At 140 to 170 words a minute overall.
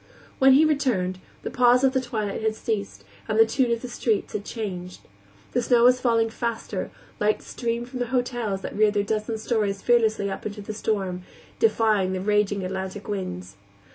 No: average, 185 wpm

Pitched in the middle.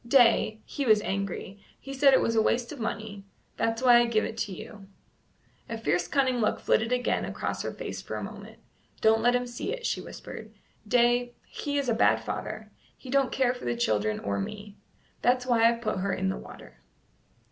No: high, 230 Hz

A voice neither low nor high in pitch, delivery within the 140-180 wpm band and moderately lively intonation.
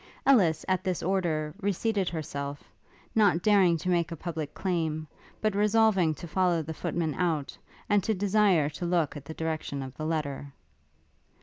Yes: medium, 170 Hz; average, 170 wpm; average, 3.7 semitones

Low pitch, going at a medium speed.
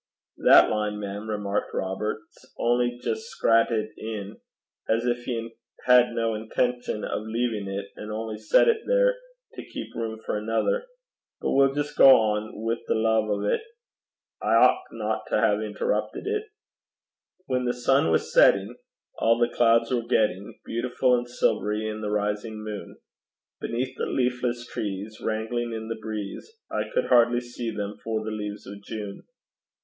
Yes: low, 115 Hz; average, 160 wpm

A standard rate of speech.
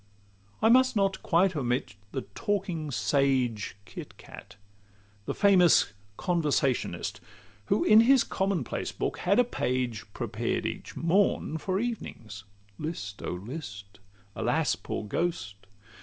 No: slow, 125 wpm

